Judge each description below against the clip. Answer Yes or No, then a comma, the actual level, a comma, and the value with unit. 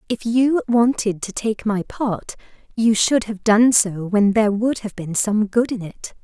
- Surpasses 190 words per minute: Yes, average, 200 wpm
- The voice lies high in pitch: Yes, high, 215 Hz